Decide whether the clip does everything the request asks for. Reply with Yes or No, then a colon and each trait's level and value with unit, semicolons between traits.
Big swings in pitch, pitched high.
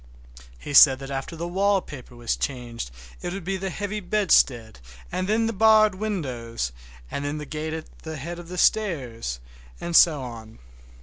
No: wide, 7.2 semitones; medium, 160 Hz